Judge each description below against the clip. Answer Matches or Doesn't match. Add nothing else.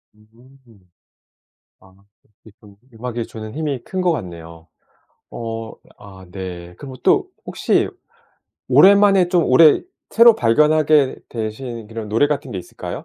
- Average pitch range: Doesn't match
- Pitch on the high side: Doesn't match